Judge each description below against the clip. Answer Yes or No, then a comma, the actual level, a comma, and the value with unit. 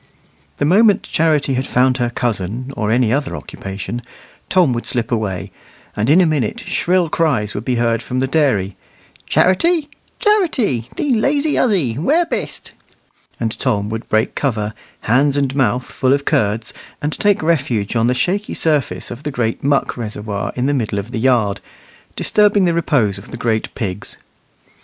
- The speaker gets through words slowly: No, average, 170 wpm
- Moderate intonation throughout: No, wide, 6.3 semitones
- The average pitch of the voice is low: Yes, low, 130 Hz